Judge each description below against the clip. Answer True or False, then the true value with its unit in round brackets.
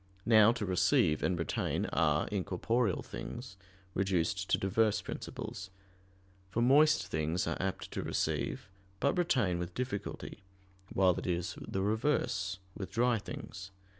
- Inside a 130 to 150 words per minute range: True (135 wpm)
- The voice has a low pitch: True (95 Hz)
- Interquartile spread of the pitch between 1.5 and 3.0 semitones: False (4.1 semitones)